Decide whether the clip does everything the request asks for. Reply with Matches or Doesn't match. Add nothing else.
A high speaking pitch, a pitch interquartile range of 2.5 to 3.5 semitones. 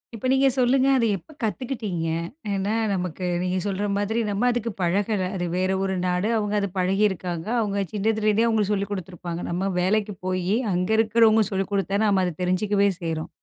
Matches